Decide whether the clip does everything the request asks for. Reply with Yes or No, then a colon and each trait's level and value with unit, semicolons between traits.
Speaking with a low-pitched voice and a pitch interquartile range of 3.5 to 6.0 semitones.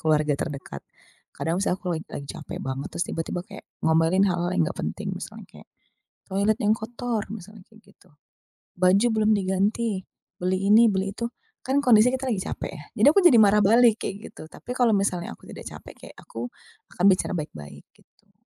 No: high, 195 Hz; average, 4.1 semitones